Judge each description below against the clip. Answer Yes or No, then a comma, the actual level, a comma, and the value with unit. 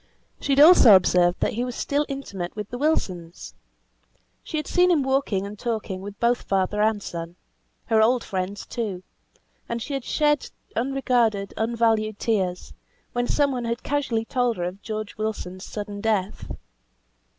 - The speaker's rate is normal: Yes, average, 160 wpm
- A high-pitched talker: Yes, high, 220 Hz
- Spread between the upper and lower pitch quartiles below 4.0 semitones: No, average, 4.3 semitones